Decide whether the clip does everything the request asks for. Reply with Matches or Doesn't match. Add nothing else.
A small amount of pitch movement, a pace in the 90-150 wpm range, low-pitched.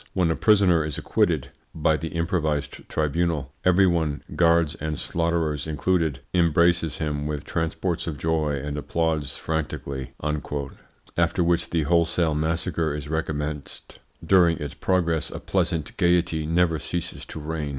Matches